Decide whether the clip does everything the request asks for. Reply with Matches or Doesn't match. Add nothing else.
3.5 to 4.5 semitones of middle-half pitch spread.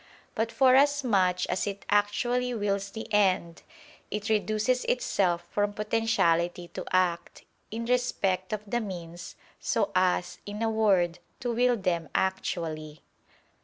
Matches